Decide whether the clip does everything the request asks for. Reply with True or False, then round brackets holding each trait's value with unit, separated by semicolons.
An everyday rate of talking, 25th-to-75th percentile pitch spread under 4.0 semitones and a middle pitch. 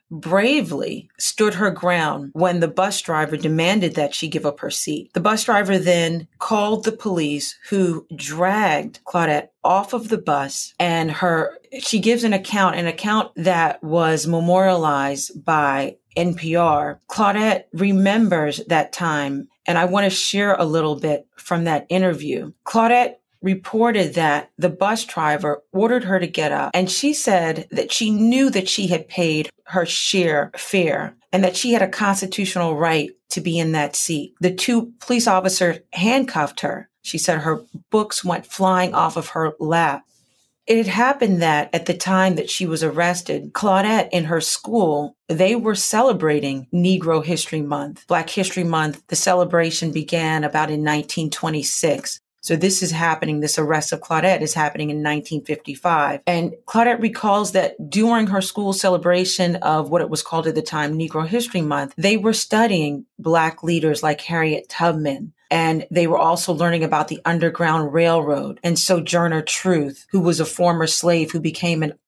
True (165 wpm; 3.4 semitones; 175 Hz)